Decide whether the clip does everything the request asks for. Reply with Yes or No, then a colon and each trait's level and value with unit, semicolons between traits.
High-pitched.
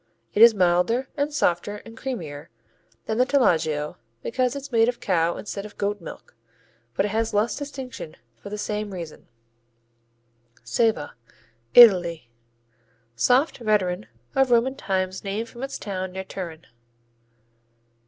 Yes: high, 210 Hz